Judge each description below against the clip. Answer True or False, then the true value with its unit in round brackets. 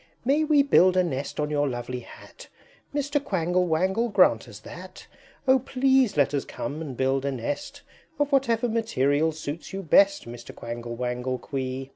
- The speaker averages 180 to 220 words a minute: False (170 wpm)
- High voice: False (160 Hz)